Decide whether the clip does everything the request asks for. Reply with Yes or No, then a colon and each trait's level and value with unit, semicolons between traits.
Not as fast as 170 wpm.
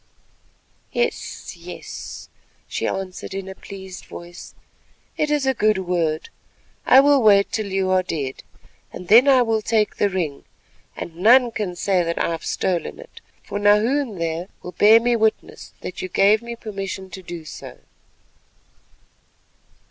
Yes: average, 155 wpm